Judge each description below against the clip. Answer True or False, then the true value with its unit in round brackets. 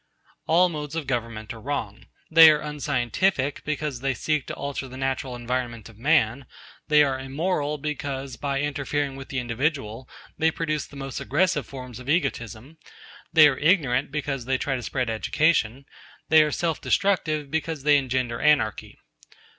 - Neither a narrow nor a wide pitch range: True (3.2 semitones)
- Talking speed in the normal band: True (160 wpm)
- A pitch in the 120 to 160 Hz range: True (140 Hz)